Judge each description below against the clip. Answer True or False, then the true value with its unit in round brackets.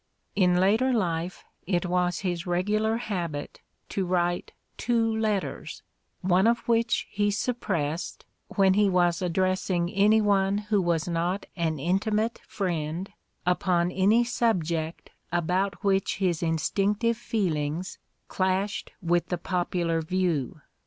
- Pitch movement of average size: True (3.1 semitones)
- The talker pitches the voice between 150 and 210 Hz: True (185 Hz)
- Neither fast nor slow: False (120 wpm)